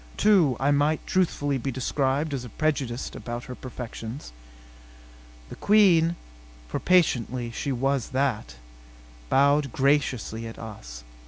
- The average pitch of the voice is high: No, low, 135 Hz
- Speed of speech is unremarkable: No, slow, 115 wpm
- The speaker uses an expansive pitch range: No, average, 3.7 semitones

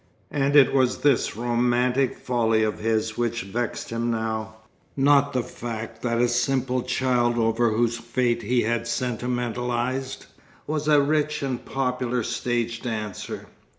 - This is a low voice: Yes, low, 120 Hz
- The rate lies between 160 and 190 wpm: No, average, 140 wpm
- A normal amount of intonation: No, narrow, 1.8 semitones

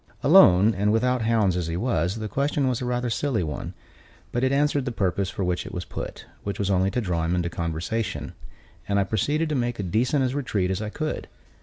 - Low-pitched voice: Yes, low, 110 Hz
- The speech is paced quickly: Yes, fast, 225 wpm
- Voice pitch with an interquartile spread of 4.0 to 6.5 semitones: Yes, wide, 5.6 semitones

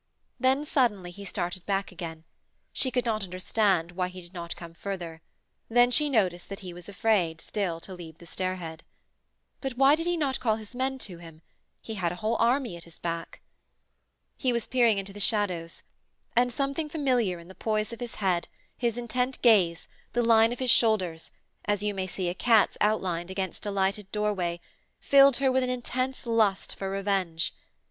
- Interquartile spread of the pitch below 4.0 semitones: No, wide, 5.4 semitones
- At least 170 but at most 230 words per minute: Yes, average, 190 wpm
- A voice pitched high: Yes, high, 205 Hz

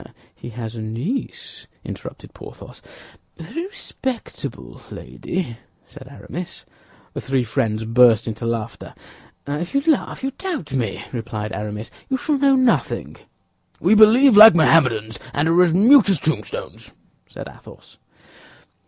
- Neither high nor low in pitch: Yes, medium, 150 Hz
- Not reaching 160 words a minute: Yes, average, 145 wpm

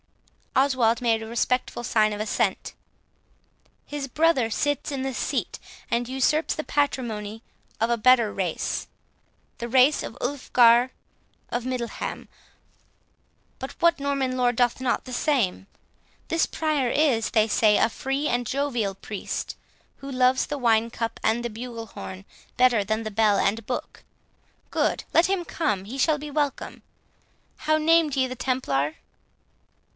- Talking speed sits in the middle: Yes, average, 145 wpm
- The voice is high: Yes, very high, 250 Hz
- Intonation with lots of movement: No, average, 3.7 semitones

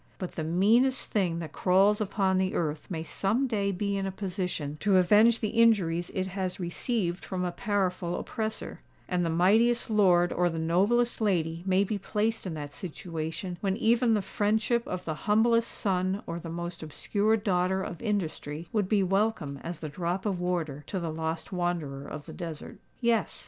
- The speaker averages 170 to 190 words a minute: Yes, average, 185 wpm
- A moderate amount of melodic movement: Yes, average, 3.6 semitones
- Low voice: No, medium, 185 Hz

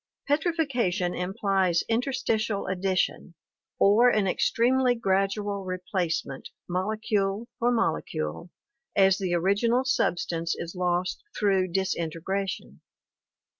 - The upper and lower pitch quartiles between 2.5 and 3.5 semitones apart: No, average, 3.9 semitones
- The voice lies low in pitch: No, high, 195 Hz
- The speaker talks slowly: Yes, slow, 95 wpm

